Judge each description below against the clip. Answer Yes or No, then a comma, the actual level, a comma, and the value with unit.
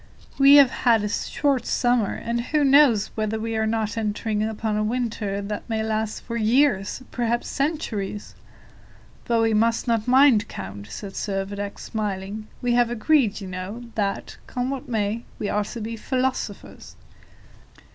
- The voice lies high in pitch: Yes, high, 220 Hz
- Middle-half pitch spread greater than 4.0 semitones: No, average, 2.7 semitones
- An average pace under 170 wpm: Yes, average, 160 wpm